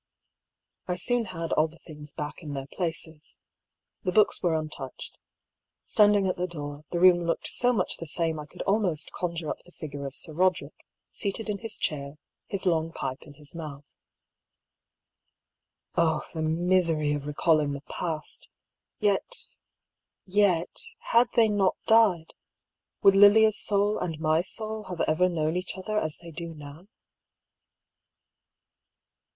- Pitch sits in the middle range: Yes, medium, 170 Hz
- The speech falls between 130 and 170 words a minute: Yes, average, 150 wpm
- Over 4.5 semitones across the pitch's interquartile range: No, average, 4.2 semitones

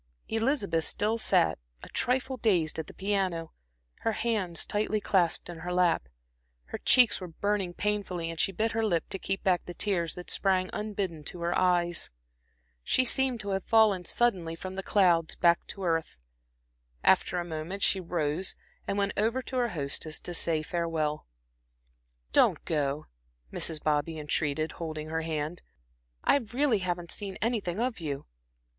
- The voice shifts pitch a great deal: No, average, 4.1 semitones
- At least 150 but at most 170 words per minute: Yes, average, 165 wpm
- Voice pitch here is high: No, medium, 180 Hz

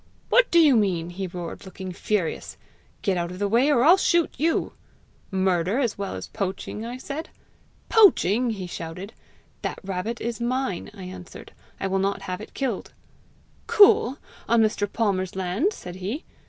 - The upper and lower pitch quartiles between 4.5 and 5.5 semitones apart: Yes, average, 5.2 semitones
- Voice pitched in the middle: No, high, 205 Hz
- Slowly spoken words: No, average, 165 wpm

